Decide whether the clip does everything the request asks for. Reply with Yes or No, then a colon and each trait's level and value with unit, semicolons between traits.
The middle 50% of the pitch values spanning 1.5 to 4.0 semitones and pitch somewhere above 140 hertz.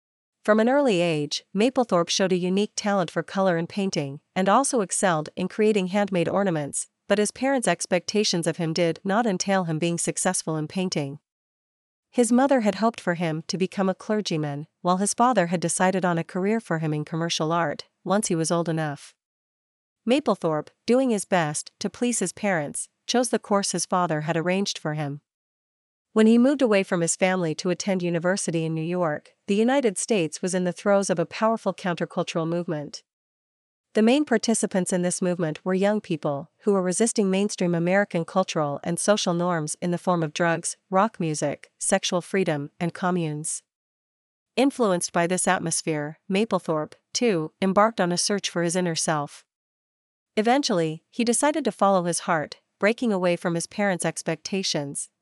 Yes: average, 3.5 semitones; medium, 185 Hz